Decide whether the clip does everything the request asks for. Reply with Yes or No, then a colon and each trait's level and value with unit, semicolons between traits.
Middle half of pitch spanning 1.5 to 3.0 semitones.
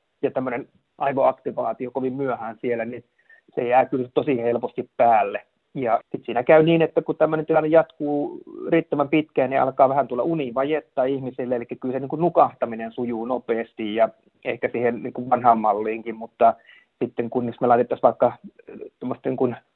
No: average, 4.7 semitones